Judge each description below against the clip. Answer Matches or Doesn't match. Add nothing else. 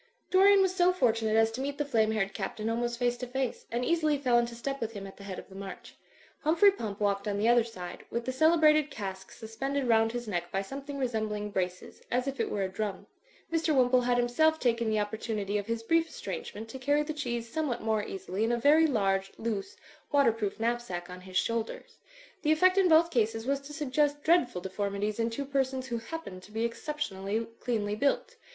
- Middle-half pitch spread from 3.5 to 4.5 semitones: Doesn't match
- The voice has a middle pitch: Doesn't match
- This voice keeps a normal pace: Doesn't match